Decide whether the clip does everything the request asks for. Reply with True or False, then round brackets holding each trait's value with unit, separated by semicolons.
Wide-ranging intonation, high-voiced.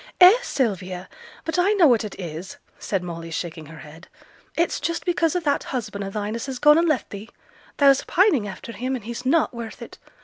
True (8.3 semitones; 235 Hz)